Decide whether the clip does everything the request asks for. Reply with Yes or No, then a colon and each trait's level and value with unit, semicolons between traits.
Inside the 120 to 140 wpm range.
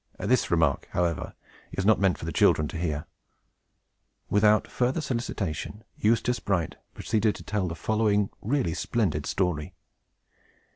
Yes: slow, 135 wpm